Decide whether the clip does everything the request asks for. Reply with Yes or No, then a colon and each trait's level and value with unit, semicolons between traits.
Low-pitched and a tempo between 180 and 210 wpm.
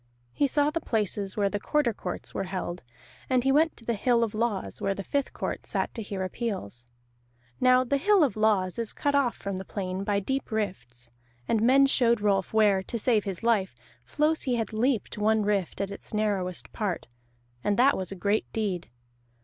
No: high, 215 Hz; average, 200 wpm